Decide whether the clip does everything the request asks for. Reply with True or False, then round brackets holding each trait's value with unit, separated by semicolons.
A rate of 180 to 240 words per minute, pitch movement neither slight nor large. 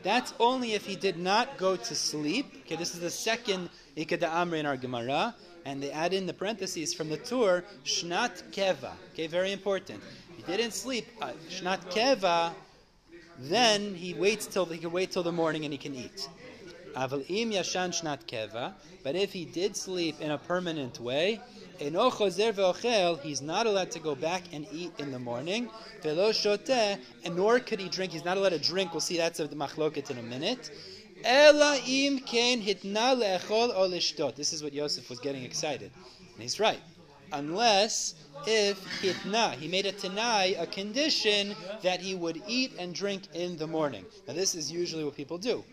False (165 wpm; 4.6 semitones)